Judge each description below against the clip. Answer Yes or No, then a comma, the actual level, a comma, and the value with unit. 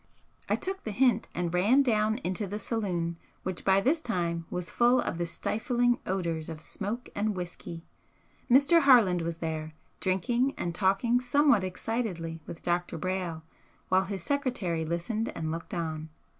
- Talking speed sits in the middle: Yes, average, 155 wpm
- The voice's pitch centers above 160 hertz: Yes, high, 190 Hz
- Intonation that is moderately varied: No, wide, 5.9 semitones